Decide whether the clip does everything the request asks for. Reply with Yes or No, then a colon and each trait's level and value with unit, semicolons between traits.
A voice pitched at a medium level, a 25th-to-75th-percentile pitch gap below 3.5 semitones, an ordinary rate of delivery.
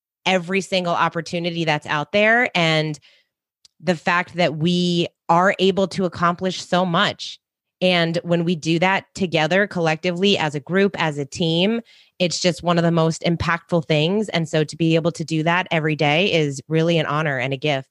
Yes: medium, 170 Hz; narrow, 2.4 semitones; average, 185 wpm